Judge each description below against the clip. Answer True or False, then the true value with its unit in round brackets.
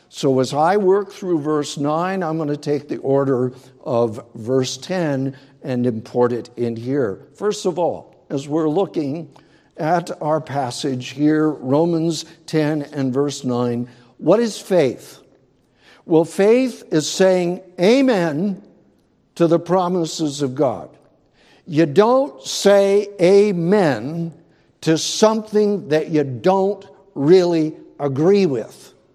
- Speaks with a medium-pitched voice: True (160 Hz)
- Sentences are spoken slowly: True (125 wpm)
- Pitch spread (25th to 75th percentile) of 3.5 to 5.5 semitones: True (5.1 semitones)